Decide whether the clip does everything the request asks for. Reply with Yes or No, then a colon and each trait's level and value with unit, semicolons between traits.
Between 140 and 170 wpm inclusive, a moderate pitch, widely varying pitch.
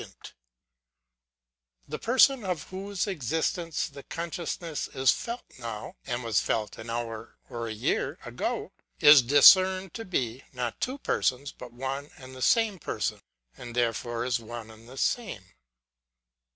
No: average, 145 wpm; low, 130 Hz; wide, 7.5 semitones